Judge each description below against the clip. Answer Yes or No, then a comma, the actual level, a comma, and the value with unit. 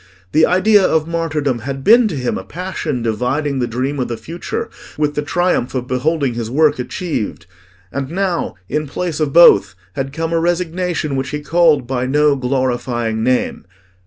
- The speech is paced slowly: No, average, 175 wpm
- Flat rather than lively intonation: No, average, 4.7 semitones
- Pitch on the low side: No, medium, 145 Hz